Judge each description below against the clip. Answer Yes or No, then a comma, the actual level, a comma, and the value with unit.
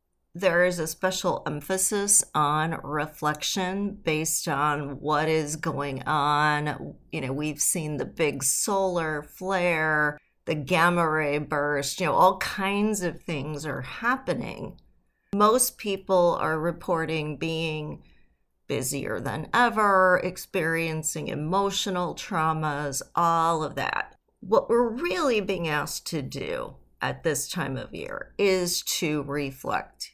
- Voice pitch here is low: No, medium, 160 Hz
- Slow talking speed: Yes, slow, 125 wpm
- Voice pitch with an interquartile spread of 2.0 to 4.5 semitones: Yes, average, 3.9 semitones